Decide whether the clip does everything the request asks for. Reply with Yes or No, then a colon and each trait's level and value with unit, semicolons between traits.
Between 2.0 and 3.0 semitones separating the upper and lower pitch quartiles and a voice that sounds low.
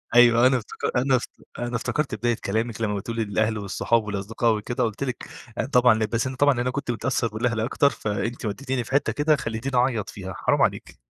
Yes: average, 2.7 semitones; low, 120 Hz